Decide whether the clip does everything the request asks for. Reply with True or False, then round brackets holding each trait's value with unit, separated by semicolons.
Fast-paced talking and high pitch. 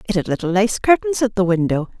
True (240 wpm; 205 Hz)